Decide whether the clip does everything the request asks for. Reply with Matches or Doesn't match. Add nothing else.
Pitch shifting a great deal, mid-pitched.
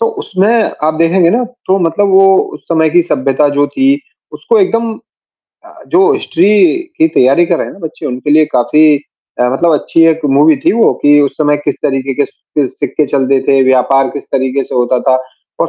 Matches